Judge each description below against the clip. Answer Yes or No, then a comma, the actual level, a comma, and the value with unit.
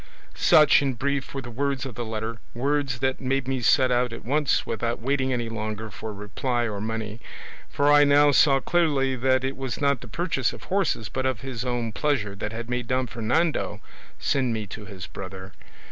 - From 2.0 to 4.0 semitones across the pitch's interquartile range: Yes, average, 3.5 semitones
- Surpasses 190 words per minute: Yes, average, 200 wpm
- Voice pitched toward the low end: Yes, low, 125 Hz